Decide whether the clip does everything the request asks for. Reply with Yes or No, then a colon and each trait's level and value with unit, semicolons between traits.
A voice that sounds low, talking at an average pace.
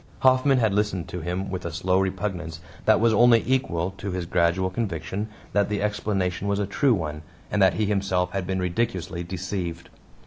Yes: very low, 95 Hz; average, 185 wpm